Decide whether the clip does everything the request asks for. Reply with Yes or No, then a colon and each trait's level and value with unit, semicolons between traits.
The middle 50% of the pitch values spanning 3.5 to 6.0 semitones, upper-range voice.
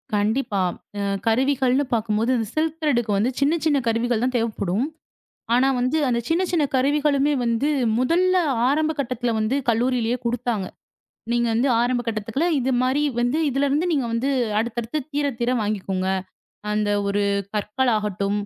Yes: average, 3.9 semitones; high, 245 Hz